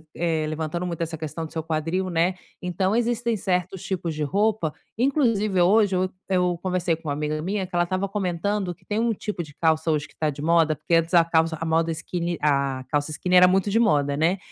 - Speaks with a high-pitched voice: No, medium, 175 Hz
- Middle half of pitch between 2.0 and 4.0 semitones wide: Yes, average, 3.1 semitones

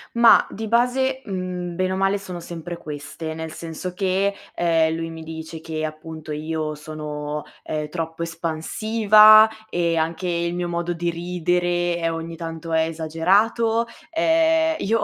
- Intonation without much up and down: No, average, 3.2 semitones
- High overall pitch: No, medium, 170 Hz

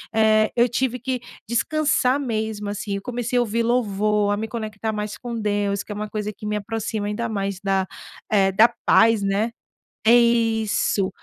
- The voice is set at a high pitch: Yes, high, 215 Hz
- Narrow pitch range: Yes, narrow, 2.3 semitones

